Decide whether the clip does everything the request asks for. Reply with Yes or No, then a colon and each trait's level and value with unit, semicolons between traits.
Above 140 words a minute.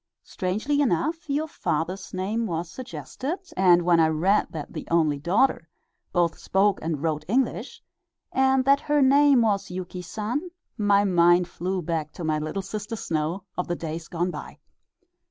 Yes: average, 160 wpm